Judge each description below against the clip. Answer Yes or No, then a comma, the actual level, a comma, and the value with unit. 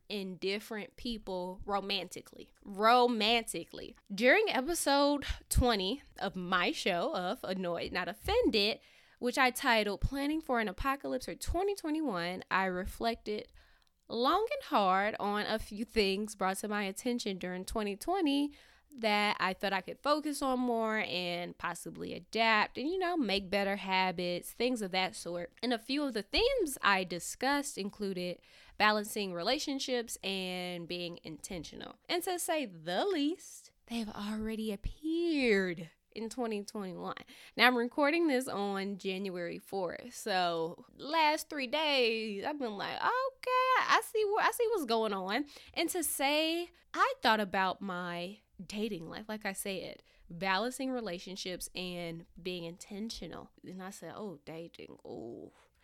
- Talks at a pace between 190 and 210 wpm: No, average, 140 wpm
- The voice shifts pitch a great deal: Yes, wide, 6.3 semitones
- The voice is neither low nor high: No, high, 215 Hz